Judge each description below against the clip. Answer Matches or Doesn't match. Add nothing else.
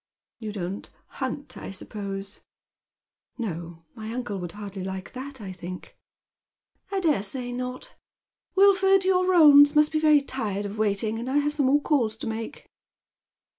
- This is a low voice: Doesn't match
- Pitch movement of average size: Doesn't match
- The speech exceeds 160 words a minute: Matches